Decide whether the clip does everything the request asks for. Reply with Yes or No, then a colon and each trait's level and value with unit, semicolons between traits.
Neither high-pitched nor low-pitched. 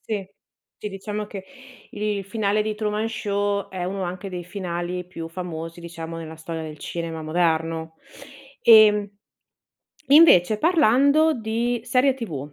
No: high, 195 Hz